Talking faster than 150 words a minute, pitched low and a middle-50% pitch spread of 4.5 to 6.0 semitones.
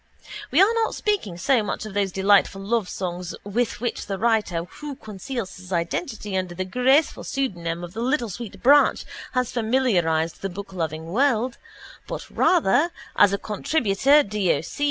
No: average, 160 wpm; high, 210 Hz; wide, 5.5 semitones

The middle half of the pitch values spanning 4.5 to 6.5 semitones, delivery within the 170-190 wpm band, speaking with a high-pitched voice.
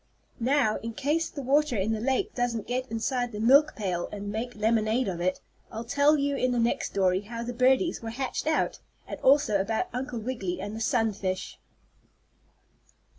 No: average, 3.8 semitones; average, 180 wpm; high, 235 Hz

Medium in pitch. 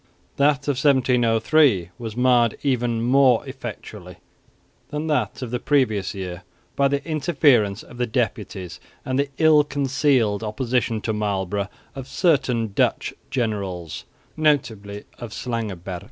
No: low, 120 Hz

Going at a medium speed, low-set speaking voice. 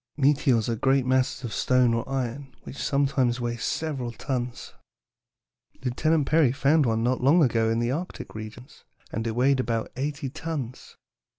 Yes: average, 160 wpm; low, 130 Hz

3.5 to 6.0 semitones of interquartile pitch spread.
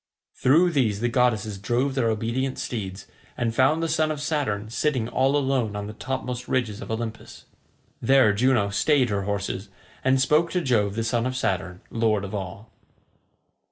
Yes: average, 4.3 semitones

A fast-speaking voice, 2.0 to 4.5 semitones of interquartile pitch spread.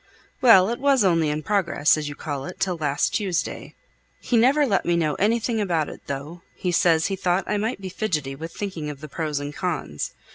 No: fast, 215 wpm; average, 5.3 semitones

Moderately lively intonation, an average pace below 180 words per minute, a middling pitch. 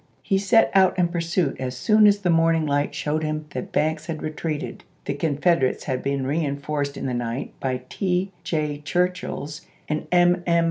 No: average, 3.7 semitones; average, 185 wpm; medium, 155 Hz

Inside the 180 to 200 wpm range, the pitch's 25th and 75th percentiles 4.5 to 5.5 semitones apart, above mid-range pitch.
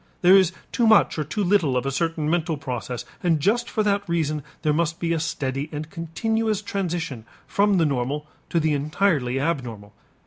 No: average, 185 wpm; average, 5.0 semitones; medium, 165 Hz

